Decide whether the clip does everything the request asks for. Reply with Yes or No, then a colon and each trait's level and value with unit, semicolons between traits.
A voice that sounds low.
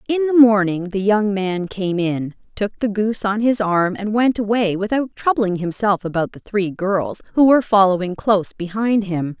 No: high, 205 Hz